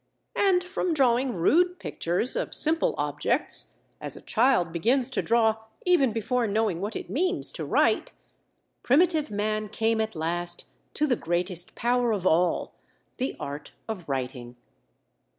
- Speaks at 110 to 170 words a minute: Yes, average, 140 wpm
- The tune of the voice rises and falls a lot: Yes, wide, 7.2 semitones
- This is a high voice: Yes, high, 225 Hz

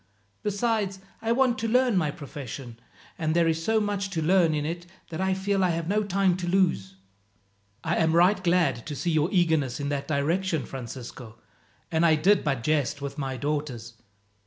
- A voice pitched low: No, medium, 165 Hz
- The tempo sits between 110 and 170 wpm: No, average, 185 wpm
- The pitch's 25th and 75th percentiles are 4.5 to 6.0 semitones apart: Yes, average, 4.9 semitones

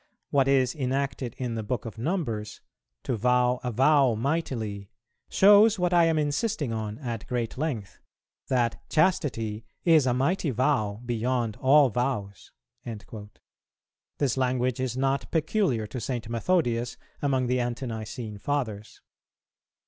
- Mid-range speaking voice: No, low, 125 Hz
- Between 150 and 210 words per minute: No, slow, 135 wpm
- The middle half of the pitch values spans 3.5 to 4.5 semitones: Yes, average, 4.0 semitones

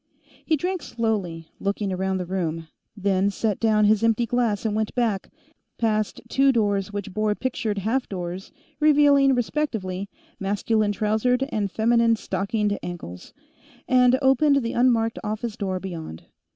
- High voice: Yes, high, 215 Hz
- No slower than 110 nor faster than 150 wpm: Yes, average, 140 wpm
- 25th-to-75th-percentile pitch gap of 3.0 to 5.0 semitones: Yes, average, 3.7 semitones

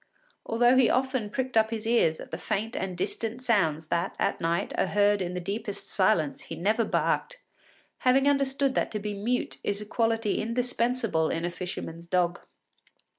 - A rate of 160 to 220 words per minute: Yes, average, 180 wpm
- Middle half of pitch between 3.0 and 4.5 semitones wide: No, average, 5.0 semitones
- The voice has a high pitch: Yes, high, 215 Hz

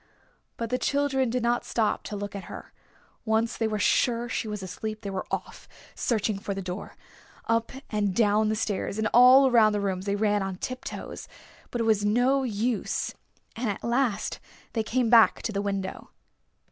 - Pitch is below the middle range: No, high, 220 Hz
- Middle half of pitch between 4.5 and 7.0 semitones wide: No, average, 2.8 semitones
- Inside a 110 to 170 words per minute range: No, average, 185 wpm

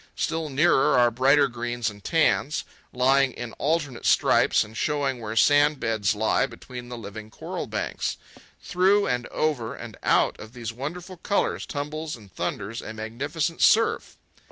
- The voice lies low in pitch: Yes, low, 130 Hz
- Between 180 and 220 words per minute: No, average, 150 wpm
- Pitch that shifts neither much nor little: Yes, average, 4.9 semitones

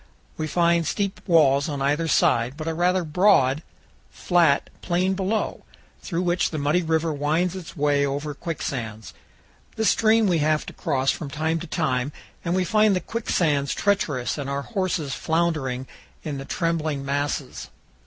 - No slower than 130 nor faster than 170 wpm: Yes, average, 160 wpm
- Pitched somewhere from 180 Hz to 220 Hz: No, medium, 160 Hz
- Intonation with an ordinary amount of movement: Yes, average, 3.9 semitones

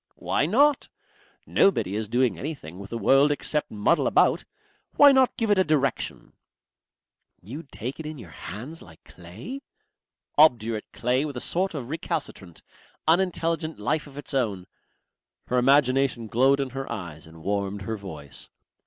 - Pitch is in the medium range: No, low, 130 Hz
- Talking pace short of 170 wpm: Yes, average, 155 wpm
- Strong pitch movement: Yes, wide, 7.1 semitones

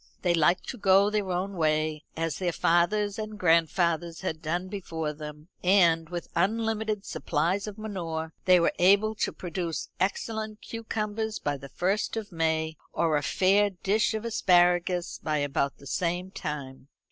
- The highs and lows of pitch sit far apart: No, average, 4.2 semitones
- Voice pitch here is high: No, medium, 180 Hz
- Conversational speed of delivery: Yes, average, 160 wpm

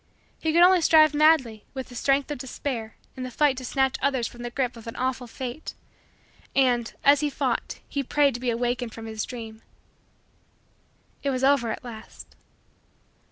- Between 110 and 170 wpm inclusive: No, average, 180 wpm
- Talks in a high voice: Yes, very high, 255 Hz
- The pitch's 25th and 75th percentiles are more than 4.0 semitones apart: No, average, 2.9 semitones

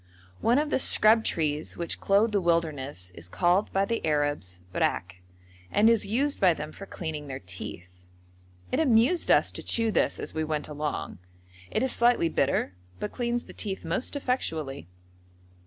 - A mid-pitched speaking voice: Yes, medium, 170 Hz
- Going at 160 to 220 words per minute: Yes, average, 170 wpm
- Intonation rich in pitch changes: Yes, wide, 7.6 semitones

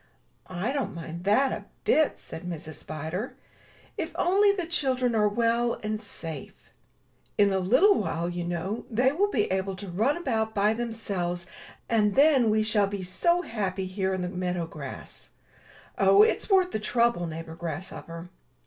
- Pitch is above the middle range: Yes, high, 210 Hz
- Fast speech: No, average, 165 wpm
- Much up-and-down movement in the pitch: Yes, wide, 5.7 semitones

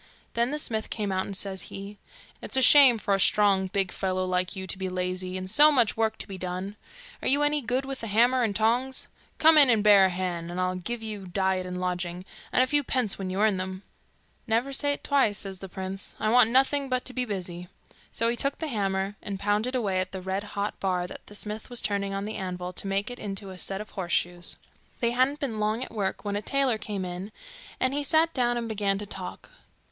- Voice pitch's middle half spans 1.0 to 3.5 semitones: No, average, 4.4 semitones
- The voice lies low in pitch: No, high, 205 Hz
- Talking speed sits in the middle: No, fast, 235 wpm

